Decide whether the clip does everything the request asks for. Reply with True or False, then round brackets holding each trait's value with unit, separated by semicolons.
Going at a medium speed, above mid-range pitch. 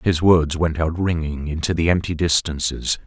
False (175 wpm; 80 Hz)